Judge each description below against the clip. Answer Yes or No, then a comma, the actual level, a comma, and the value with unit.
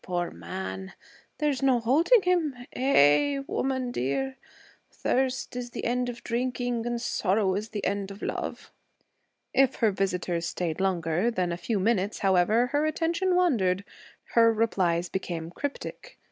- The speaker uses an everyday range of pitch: No, wide, 6.3 semitones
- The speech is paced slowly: No, average, 145 wpm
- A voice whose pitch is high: Yes, high, 225 Hz